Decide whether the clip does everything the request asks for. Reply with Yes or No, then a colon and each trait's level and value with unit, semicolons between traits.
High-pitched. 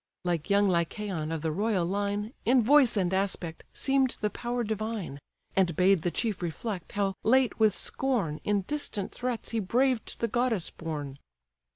Yes: high, 205 Hz